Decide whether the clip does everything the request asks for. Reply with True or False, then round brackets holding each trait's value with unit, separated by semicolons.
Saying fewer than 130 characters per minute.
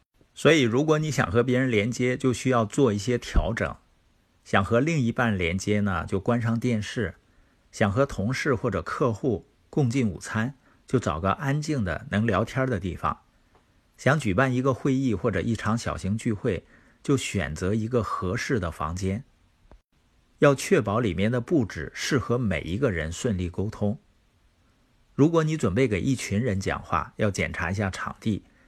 False (245 characters per minute)